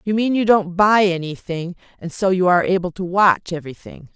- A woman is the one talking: Yes, female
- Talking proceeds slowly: No, average, 200 wpm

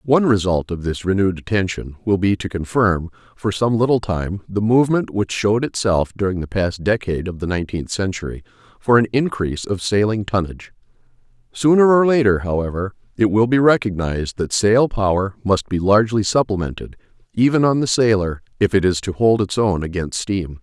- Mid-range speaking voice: No, low, 100 Hz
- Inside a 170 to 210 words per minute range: Yes, average, 175 wpm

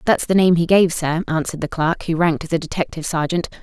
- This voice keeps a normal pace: No, fast, 250 wpm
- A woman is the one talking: Yes, female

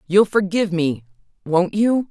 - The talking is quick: No, slow, 115 wpm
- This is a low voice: No, medium, 185 Hz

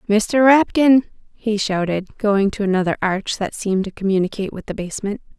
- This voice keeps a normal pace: Yes, average, 165 wpm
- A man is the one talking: No, female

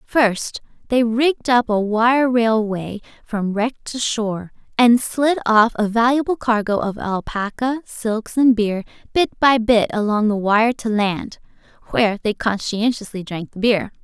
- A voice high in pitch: Yes, high, 225 Hz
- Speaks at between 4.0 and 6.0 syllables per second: No, 3.5 syllables/s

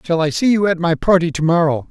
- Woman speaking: No, male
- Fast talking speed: Yes, fast, 250 wpm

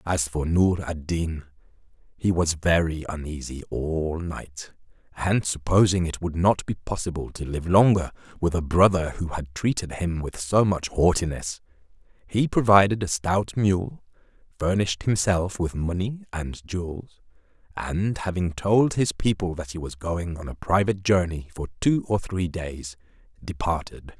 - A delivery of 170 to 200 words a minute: No, average, 155 wpm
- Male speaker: Yes, male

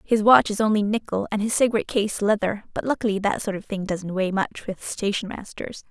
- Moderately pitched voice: No, high, 210 Hz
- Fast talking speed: Yes, fast, 225 wpm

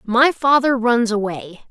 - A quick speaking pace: No, average, 140 wpm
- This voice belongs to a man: No, female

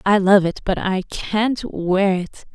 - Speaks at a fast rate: No, average, 190 wpm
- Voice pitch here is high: Yes, high, 195 Hz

